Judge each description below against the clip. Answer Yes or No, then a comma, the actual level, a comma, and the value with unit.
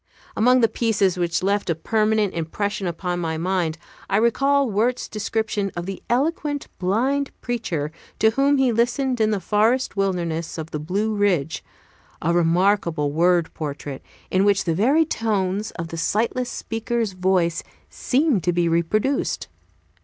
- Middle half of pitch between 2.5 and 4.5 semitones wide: No, average, 5.2 semitones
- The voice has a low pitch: No, high, 200 Hz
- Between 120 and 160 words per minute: Yes, average, 150 wpm